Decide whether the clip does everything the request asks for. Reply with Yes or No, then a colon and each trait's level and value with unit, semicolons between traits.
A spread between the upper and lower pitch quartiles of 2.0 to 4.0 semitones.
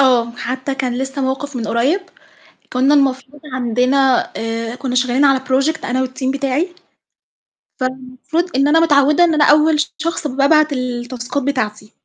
Yes: narrow, 2.4 semitones